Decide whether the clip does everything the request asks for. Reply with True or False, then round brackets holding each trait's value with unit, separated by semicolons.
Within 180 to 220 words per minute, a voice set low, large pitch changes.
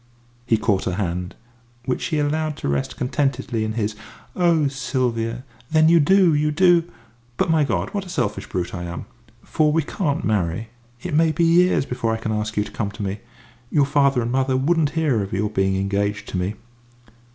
True (195 wpm; 130 Hz; 7.0 semitones)